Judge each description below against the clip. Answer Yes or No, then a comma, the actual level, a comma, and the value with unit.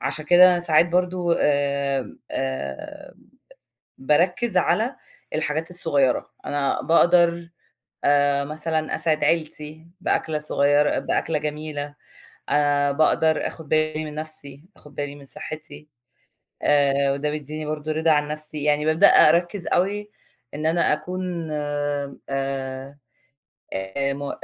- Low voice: No, medium, 150 Hz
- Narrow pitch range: Yes, narrow, 2.1 semitones